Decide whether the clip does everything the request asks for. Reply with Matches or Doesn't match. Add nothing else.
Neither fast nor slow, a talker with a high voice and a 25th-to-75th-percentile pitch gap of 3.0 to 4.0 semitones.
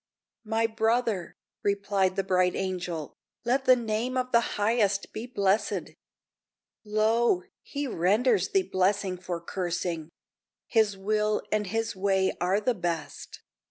Doesn't match